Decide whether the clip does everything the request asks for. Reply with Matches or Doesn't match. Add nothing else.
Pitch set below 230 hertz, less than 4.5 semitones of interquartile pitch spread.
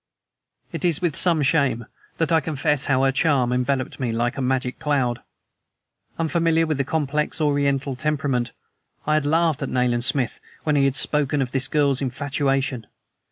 Matches